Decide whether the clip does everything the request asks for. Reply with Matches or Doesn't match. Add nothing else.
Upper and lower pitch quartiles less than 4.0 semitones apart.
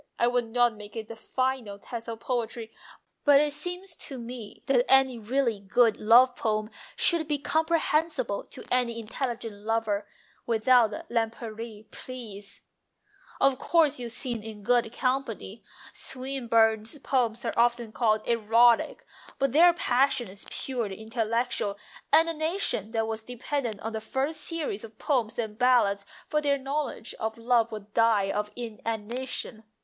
Matches